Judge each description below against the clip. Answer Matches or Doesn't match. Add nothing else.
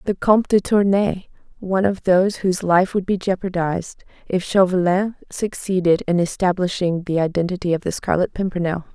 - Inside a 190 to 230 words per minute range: Doesn't match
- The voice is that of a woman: Matches